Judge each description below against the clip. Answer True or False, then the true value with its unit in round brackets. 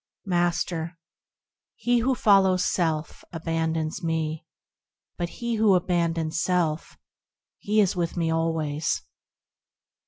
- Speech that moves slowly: True (105 wpm)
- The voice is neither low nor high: True (170 Hz)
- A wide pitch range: False (2.4 semitones)